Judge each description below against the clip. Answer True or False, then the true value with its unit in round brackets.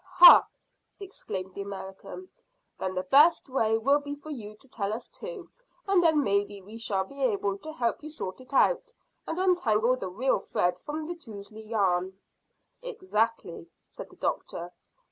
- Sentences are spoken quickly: False (165 wpm)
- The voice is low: False (230 Hz)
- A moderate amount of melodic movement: False (7.6 semitones)